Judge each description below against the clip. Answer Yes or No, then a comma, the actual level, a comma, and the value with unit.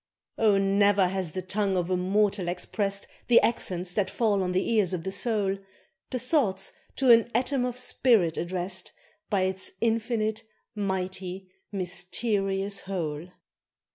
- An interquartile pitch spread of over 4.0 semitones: No, average, 2.7 semitones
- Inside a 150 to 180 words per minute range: No, average, 140 wpm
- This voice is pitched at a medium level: No, high, 195 Hz